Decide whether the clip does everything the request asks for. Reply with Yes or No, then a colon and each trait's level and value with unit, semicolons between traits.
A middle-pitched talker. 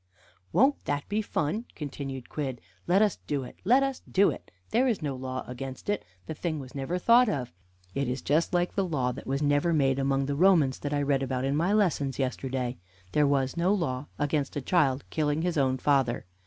Yes: medium, 145 Hz